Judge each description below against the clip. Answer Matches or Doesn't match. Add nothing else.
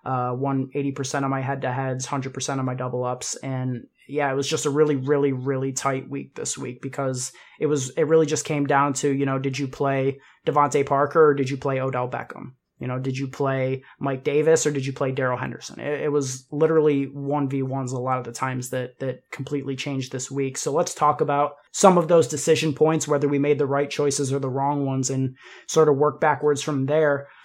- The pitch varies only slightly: Matches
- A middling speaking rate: Doesn't match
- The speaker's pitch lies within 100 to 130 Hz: Doesn't match